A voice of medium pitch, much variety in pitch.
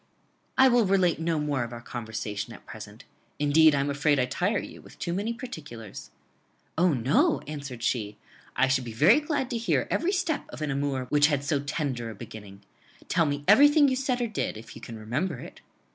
Yes: medium, 145 Hz; wide, 8.3 semitones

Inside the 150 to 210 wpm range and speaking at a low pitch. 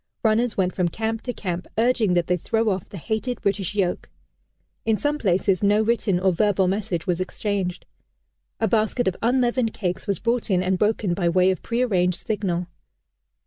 No: average, 180 wpm; high, 200 Hz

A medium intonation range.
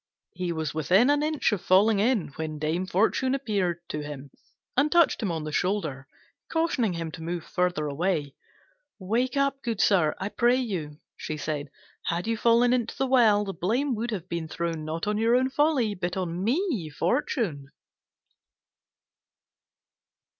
No: wide, 6.9 semitones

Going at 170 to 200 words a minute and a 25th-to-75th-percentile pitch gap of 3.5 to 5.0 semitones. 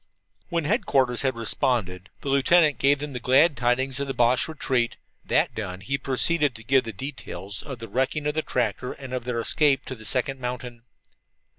No: average, 190 wpm; average, 2.9 semitones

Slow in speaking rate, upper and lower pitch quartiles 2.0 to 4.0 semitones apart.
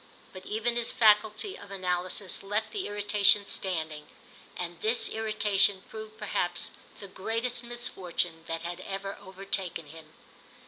Yes: slow, 130 wpm; average, 3.4 semitones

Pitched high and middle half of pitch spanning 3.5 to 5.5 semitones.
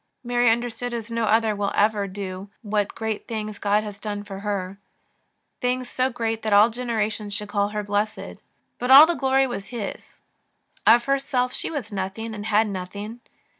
No: high, 215 Hz; average, 2.8 semitones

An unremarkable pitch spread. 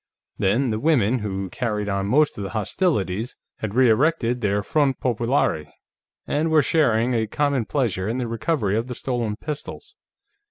Yes: average, 5.0 semitones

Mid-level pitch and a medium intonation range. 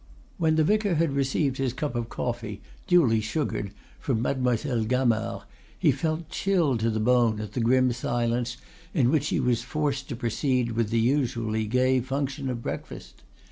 No: low, 125 Hz; average, 3.4 semitones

